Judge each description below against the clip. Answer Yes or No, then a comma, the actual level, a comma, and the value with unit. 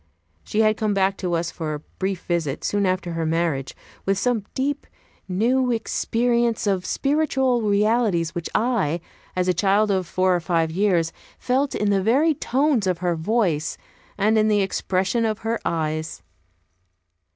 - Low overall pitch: No, high, 195 Hz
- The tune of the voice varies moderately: Yes, average, 4.9 semitones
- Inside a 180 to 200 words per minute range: No, average, 160 wpm